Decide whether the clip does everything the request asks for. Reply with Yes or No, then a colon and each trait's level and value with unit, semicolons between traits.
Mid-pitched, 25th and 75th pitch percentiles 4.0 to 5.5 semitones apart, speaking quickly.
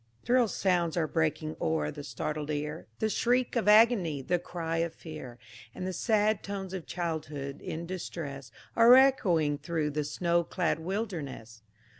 No: medium, 170 Hz; average, 4.5 semitones; average, 155 wpm